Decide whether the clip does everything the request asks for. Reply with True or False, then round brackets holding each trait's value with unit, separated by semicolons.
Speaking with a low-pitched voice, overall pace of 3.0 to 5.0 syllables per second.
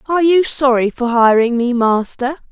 False (255 Hz; 4.9 syllables/s)